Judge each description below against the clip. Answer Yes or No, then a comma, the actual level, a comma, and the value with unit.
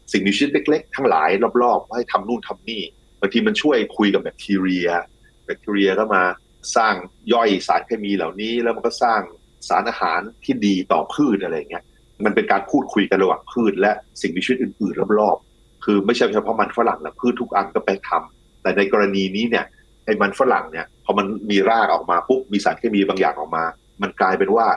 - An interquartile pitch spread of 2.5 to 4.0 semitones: Yes, average, 3.4 semitones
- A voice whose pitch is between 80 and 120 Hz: Yes, low, 100 Hz